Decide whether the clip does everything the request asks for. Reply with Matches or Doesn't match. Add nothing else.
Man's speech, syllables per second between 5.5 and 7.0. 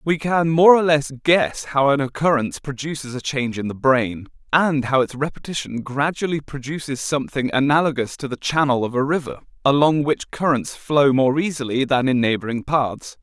Doesn't match